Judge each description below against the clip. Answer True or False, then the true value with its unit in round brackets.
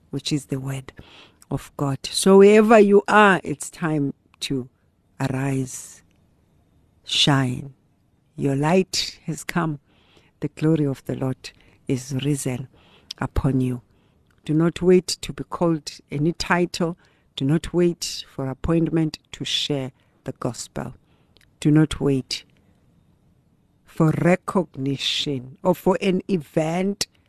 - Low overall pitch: False (145 Hz)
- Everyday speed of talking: False (120 wpm)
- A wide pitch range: False (4.5 semitones)